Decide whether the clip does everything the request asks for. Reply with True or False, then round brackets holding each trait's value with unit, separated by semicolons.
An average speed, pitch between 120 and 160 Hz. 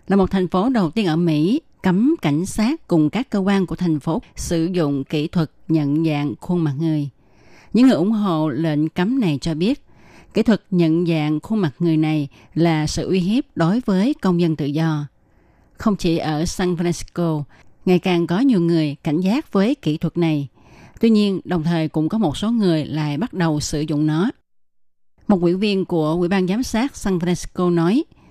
False (205 wpm; 170 Hz)